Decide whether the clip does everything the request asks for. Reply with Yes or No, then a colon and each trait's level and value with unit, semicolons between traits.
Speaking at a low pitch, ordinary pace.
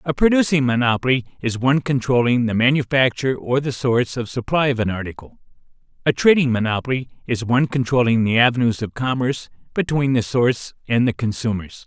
Yes: low, 125 Hz; average, 160 wpm